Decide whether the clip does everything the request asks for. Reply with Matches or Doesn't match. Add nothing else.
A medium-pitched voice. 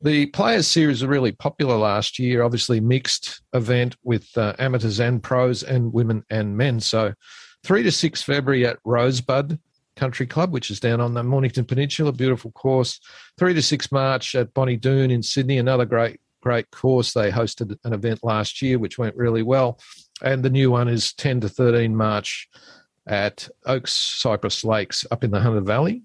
Doesn't match